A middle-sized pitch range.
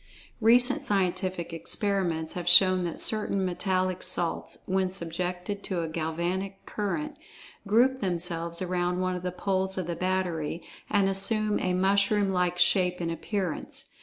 No: narrow, 2.1 semitones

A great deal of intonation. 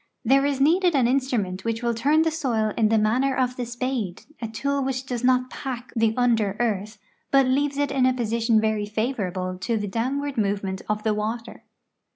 No: average, 3.6 semitones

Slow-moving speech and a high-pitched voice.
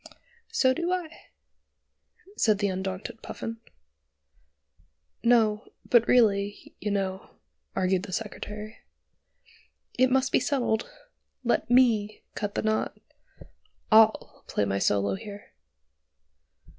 Yes: slow, 105 wpm; high, 215 Hz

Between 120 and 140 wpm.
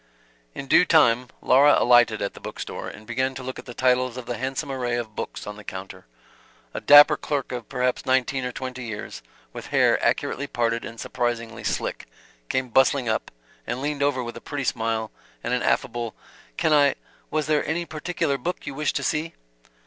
No: average, 195 wpm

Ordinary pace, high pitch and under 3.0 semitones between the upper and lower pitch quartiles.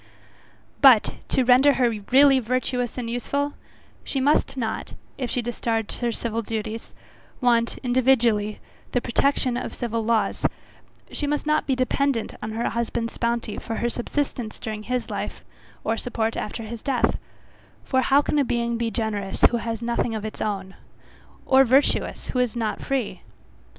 Yes: average, 160 wpm; high, 235 Hz; narrow, 2.5 semitones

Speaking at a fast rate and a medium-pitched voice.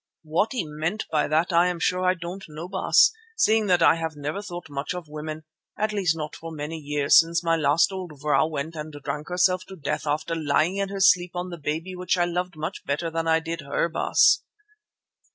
Yes: fast, 220 wpm; medium, 165 Hz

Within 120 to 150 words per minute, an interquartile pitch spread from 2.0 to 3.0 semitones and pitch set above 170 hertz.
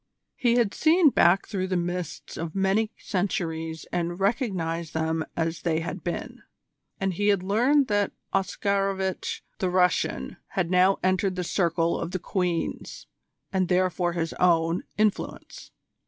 Yes: average, 140 wpm; narrow, 2.6 semitones; medium, 185 Hz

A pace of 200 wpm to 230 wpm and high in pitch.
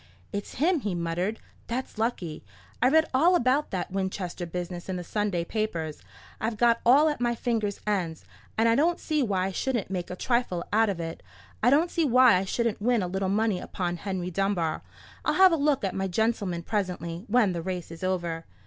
Yes: fast, 205 wpm; high, 200 Hz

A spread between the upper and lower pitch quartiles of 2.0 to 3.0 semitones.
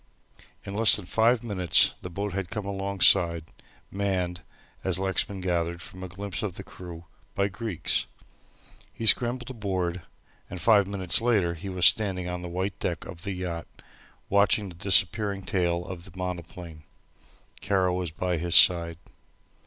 Yes: narrow, 2.4 semitones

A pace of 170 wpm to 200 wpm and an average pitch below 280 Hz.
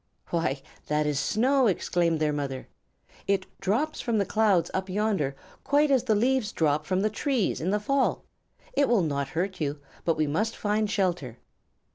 Yes: average, 175 wpm; high, 190 Hz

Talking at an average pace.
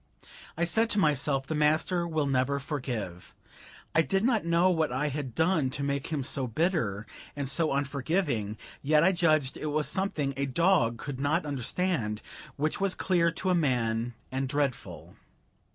Yes: average, 170 wpm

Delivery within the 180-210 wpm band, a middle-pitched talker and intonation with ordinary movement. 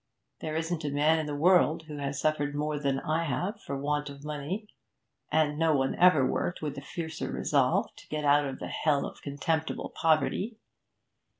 No: average, 185 wpm; medium, 150 Hz; narrow, 2.0 semitones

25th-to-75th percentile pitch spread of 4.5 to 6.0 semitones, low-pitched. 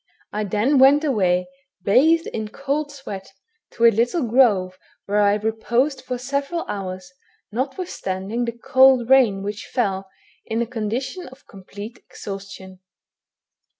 No: average, 5.0 semitones; high, 230 Hz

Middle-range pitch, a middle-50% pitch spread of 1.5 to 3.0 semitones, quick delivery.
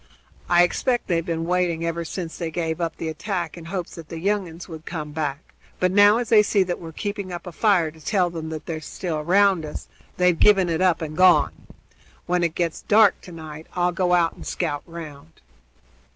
Yes: medium, 170 Hz; narrow, 2.4 semitones; fast, 220 wpm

